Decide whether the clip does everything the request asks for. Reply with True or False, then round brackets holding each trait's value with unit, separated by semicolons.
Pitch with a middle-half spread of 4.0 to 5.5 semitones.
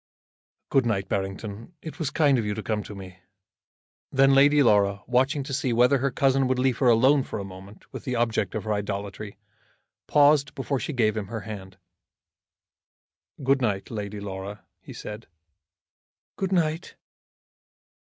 True (5.0 semitones)